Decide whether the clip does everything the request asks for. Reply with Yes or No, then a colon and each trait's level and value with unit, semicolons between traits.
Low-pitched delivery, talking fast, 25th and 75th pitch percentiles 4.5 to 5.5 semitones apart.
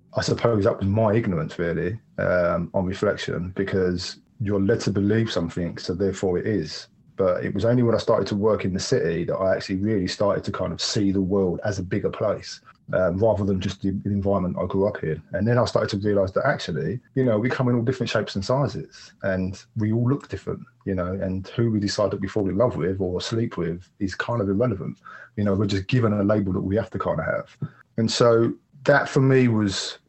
No: low, 100 Hz; fast, 235 wpm; average, 3.3 semitones